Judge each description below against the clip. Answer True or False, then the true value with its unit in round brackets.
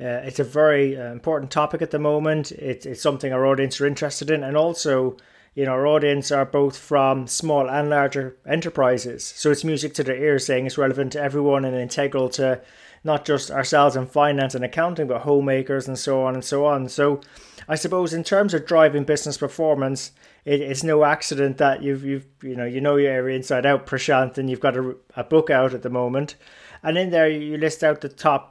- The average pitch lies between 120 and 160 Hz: True (140 Hz)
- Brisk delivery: True (215 wpm)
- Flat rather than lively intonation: True (2.2 semitones)